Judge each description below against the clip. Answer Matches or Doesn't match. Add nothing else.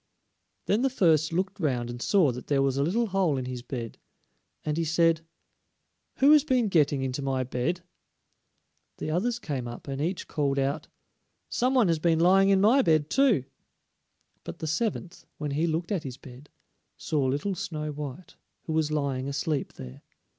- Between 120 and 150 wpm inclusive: Doesn't match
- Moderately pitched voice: Matches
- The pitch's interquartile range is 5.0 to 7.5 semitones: Matches